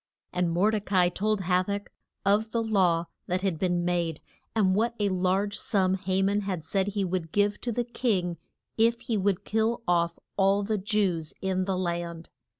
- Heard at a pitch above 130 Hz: Yes, high, 190 Hz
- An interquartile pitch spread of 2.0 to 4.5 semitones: Yes, average, 2.7 semitones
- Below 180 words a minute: No, average, 195 wpm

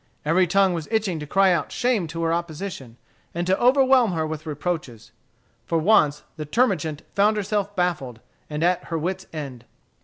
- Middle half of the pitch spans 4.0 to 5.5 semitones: Yes, average, 4.3 semitones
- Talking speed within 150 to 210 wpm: Yes, average, 175 wpm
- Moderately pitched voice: Yes, medium, 175 Hz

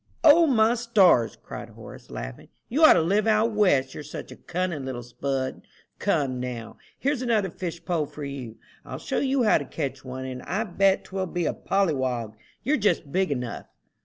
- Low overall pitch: No, medium, 170 Hz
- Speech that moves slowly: No, average, 190 wpm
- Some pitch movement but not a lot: No, wide, 8.4 semitones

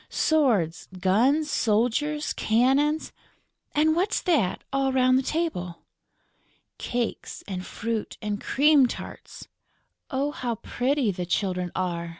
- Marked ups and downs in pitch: Yes, wide, 6.7 semitones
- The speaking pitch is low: No, very high, 250 Hz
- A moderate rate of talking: No, slow, 115 wpm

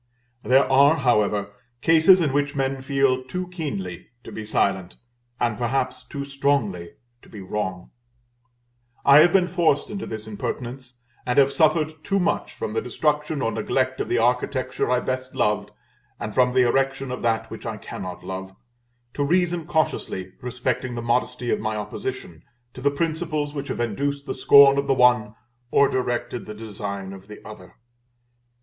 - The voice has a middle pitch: No, low, 130 Hz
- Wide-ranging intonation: No, average, 4.5 semitones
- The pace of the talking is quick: No, average, 170 wpm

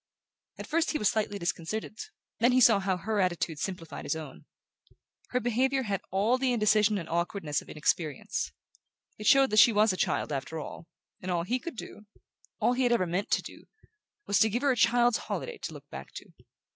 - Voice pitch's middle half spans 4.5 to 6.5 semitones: Yes, average, 5.3 semitones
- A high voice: Yes, high, 210 Hz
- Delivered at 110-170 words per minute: No, fast, 205 wpm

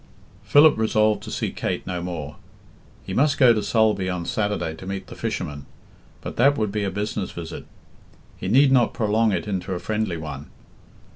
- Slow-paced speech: No, average, 185 wpm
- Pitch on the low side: Yes, low, 105 Hz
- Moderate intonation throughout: Yes, average, 3.9 semitones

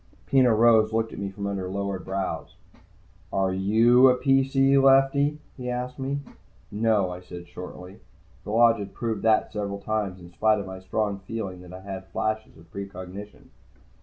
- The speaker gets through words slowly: No, average, 170 wpm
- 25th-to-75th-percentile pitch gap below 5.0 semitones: Yes, average, 3.9 semitones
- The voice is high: No, low, 105 Hz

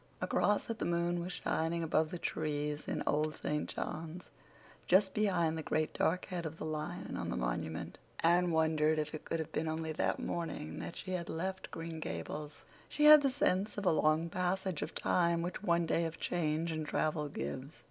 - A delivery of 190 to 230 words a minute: Yes, average, 200 wpm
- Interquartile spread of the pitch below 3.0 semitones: Yes, narrow, 2.4 semitones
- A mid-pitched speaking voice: Yes, medium, 165 Hz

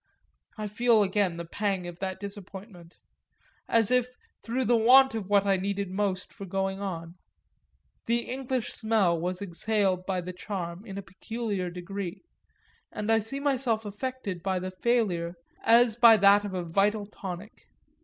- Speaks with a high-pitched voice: Yes, high, 200 Hz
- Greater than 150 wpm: Yes, average, 160 wpm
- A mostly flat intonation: No, average, 3.4 semitones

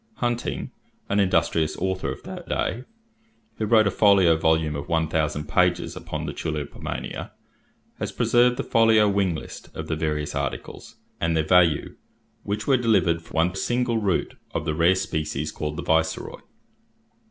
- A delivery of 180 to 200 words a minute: No, average, 165 wpm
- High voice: No, very low, 85 Hz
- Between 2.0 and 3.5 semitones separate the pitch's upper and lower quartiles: No, average, 4.7 semitones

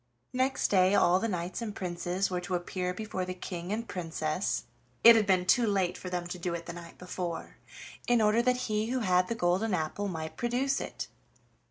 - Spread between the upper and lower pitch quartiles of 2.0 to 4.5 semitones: Yes, average, 3.7 semitones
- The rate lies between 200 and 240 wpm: Yes, fast, 205 wpm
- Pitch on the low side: No, medium, 185 Hz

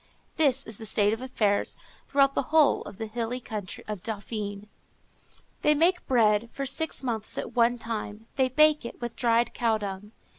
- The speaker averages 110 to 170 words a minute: No, average, 180 wpm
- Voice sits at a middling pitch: No, high, 235 Hz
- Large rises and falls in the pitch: No, average, 3.9 semitones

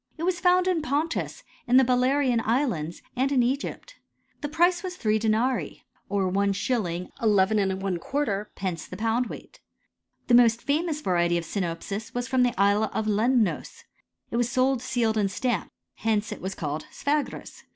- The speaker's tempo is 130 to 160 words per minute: Yes, average, 155 wpm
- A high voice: Yes, high, 230 Hz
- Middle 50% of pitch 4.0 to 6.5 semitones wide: Yes, average, 5.2 semitones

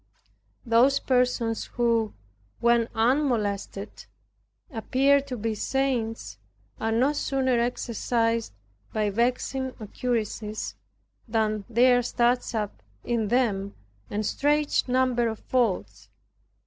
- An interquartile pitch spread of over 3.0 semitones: No, narrow, 2.6 semitones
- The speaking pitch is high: Yes, high, 235 Hz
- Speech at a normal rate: No, slow, 95 wpm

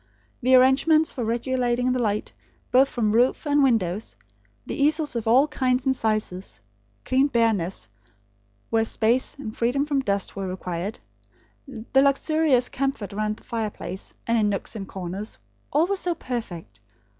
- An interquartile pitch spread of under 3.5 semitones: No, average, 4.3 semitones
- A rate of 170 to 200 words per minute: No, average, 150 wpm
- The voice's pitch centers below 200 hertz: No, high, 235 Hz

